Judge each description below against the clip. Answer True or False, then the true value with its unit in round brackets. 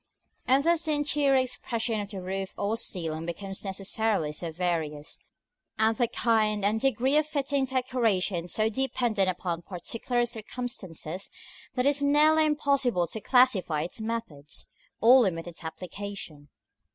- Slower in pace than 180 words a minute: True (140 wpm)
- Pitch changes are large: True (6.1 semitones)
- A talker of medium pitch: False (220 Hz)